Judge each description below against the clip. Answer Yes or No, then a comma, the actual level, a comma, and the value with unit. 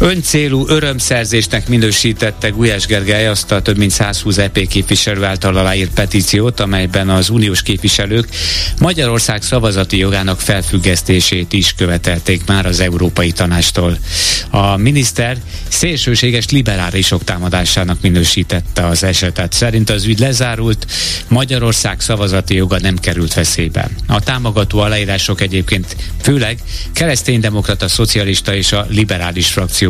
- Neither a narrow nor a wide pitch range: Yes, average, 3.8 semitones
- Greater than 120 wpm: No, average, 115 wpm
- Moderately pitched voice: No, low, 100 Hz